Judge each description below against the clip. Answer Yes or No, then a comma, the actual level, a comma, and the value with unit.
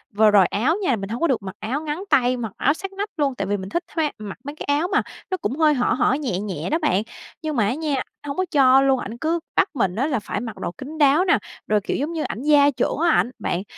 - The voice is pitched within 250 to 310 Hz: Yes, very high, 275 Hz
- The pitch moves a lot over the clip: Yes, wide, 6.1 semitones